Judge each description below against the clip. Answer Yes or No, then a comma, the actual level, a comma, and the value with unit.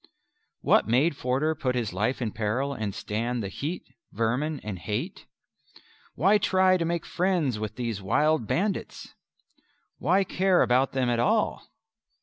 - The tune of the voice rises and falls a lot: Yes, wide, 7.1 semitones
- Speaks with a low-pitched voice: Yes, low, 130 Hz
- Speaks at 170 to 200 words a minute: No, average, 145 wpm